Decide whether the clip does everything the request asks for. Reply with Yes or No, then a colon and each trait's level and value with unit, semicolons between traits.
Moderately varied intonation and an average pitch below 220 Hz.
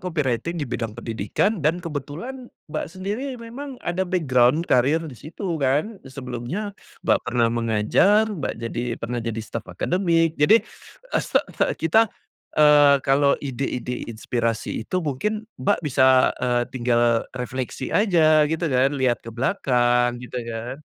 No: wide, 6.2 semitones; medium, 140 Hz